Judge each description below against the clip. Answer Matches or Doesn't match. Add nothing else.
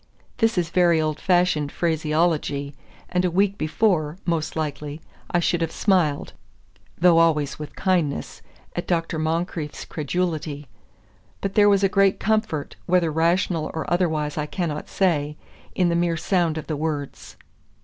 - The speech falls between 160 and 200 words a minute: Doesn't match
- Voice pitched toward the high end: Doesn't match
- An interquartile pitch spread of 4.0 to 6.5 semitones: Doesn't match